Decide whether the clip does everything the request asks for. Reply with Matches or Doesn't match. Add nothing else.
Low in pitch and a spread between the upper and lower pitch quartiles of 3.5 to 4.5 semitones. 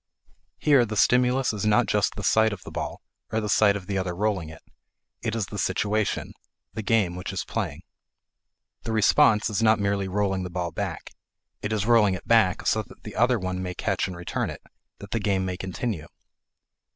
Doesn't match